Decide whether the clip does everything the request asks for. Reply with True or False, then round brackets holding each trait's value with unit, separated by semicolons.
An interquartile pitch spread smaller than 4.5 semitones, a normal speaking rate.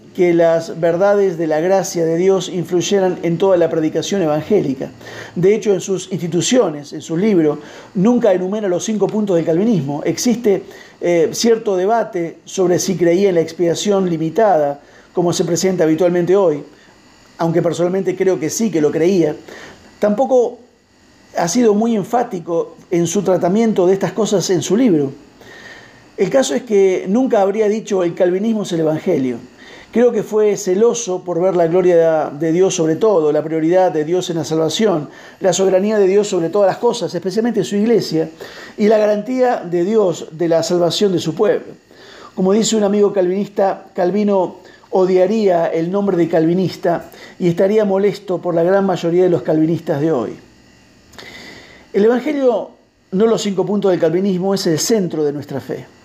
True (3.5 semitones; 170 wpm)